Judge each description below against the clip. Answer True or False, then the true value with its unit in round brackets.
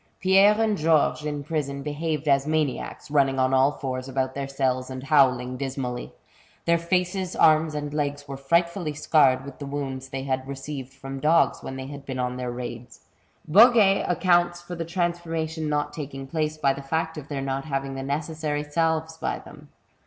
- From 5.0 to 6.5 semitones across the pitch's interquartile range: False (3.1 semitones)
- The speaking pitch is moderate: True (145 Hz)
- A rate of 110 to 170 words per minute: False (180 wpm)